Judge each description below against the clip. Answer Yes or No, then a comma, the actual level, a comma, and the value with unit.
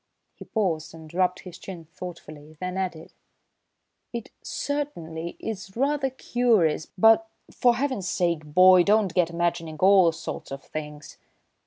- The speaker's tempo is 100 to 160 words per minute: Yes, slow, 135 wpm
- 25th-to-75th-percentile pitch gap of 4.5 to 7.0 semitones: Yes, average, 5.1 semitones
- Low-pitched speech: No, medium, 180 Hz